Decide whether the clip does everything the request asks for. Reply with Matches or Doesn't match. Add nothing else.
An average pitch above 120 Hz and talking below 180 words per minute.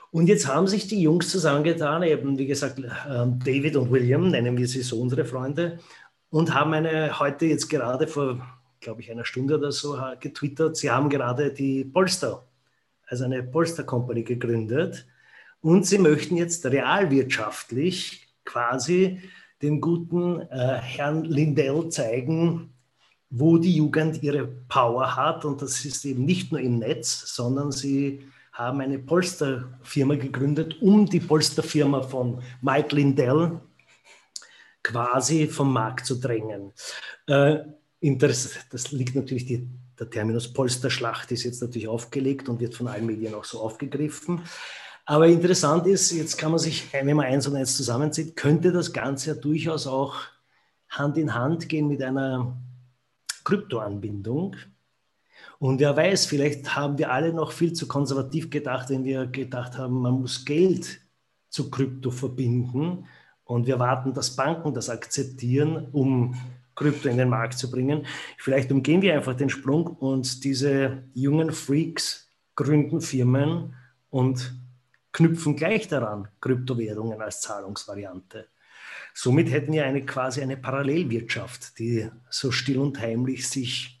Matches